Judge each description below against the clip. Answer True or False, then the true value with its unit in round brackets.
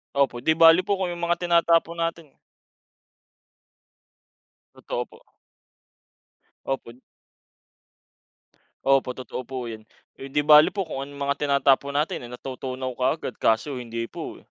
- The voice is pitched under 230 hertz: True (140 Hz)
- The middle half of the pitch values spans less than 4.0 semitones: False (4.4 semitones)